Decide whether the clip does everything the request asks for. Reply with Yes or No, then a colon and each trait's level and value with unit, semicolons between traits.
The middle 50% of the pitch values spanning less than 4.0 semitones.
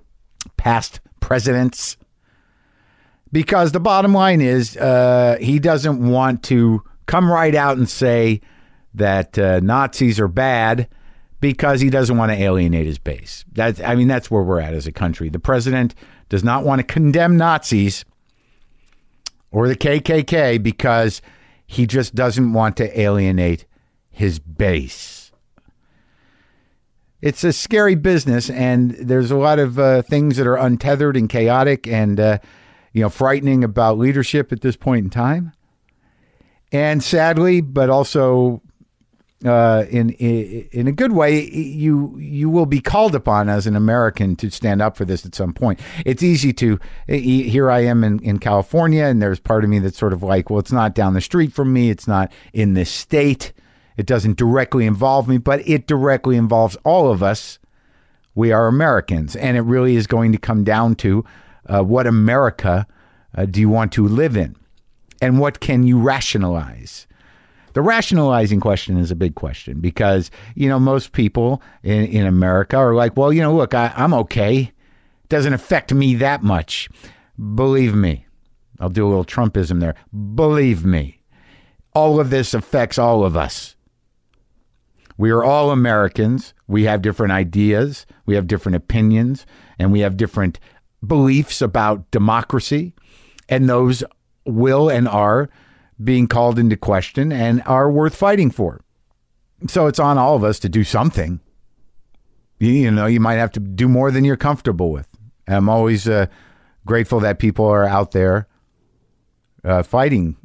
No: average, 4.8 semitones